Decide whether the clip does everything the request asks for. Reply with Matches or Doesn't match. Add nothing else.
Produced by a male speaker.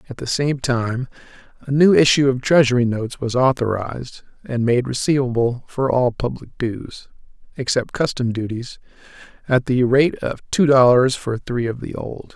Matches